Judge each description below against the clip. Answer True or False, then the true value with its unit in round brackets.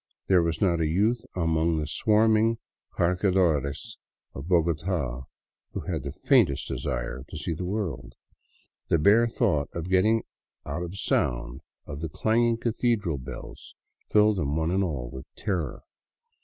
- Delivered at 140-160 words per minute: True (145 wpm)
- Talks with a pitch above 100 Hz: False (85 Hz)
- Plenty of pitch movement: True (5.8 semitones)